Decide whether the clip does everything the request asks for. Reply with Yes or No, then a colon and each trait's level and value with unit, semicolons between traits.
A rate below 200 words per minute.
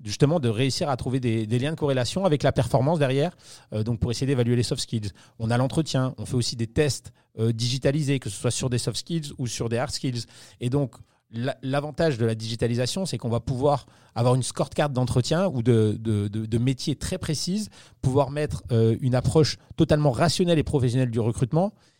No: average, 215 wpm